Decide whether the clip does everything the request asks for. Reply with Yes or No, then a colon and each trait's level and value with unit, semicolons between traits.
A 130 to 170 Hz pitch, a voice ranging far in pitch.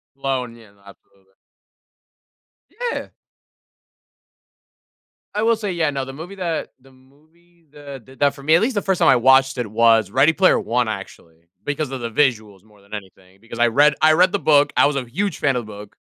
Yes: low, 135 Hz; wide, 5.7 semitones